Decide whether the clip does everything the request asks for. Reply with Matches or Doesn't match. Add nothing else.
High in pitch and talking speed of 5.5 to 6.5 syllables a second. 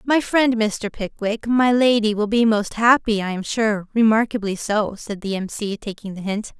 Doesn't match